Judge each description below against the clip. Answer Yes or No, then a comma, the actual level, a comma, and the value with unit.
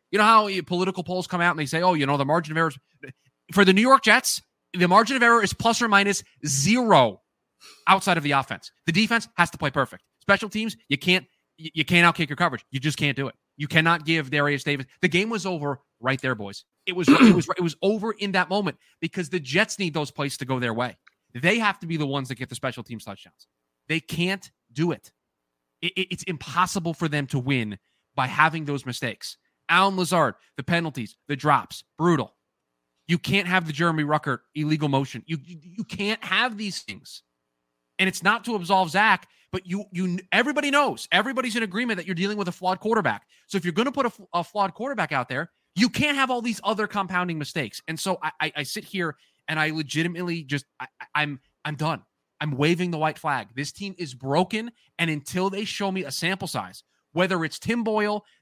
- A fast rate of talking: Yes, fast, 220 wpm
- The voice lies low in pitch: No, medium, 170 Hz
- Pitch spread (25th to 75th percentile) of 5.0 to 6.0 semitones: Yes, average, 5.3 semitones